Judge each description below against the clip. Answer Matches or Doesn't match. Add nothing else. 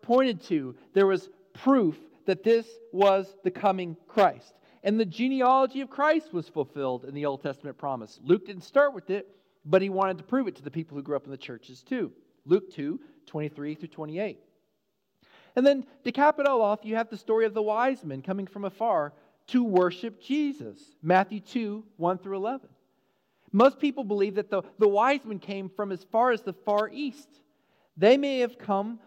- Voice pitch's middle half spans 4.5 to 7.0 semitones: Matches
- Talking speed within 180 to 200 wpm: Matches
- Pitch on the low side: Doesn't match